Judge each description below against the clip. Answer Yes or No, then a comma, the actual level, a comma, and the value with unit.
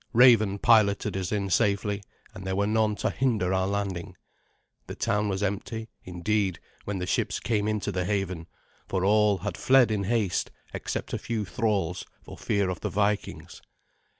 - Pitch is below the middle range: Yes, low, 100 Hz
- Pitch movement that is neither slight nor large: No, narrow, 2.2 semitones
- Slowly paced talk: No, average, 170 wpm